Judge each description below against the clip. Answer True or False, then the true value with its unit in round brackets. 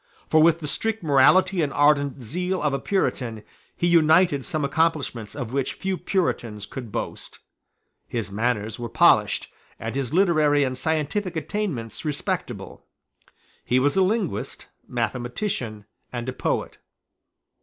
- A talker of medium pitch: True (145 Hz)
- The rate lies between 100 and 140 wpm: True (135 wpm)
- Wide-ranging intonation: True (5.8 semitones)